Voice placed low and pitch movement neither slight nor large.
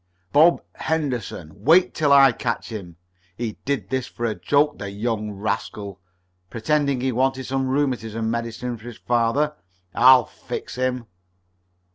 Yes: low, 125 Hz; average, 3.5 semitones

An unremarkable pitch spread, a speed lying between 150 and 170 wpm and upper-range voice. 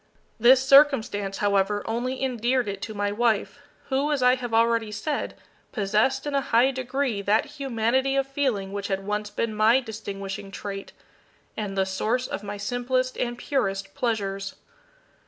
Yes: average, 4.3 semitones; average, 155 wpm; high, 230 Hz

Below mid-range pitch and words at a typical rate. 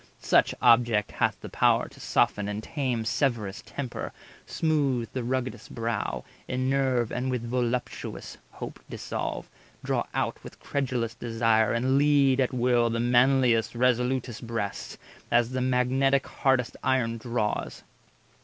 No: low, 125 Hz; slow, 130 wpm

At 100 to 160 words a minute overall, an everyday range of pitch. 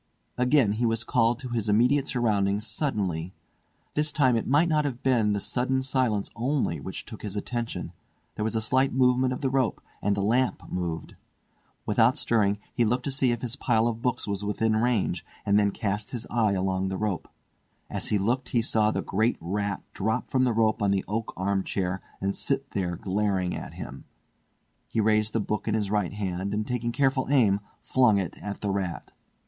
No: average, 200 wpm; average, 3.8 semitones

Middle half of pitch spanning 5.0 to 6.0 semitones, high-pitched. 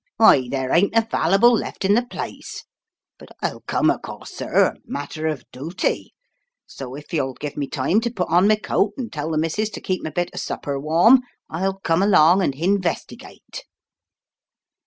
No: average, 5.3 semitones; medium, 170 Hz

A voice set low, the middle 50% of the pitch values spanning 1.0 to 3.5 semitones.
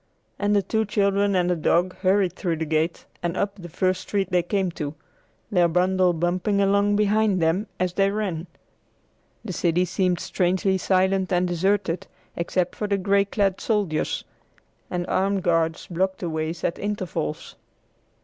No: medium, 185 Hz; narrow, 2.4 semitones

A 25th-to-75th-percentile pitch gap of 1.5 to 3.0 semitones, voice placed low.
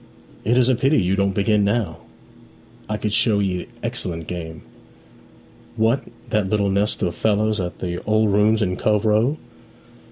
Yes: narrow, 2.5 semitones; low, 105 Hz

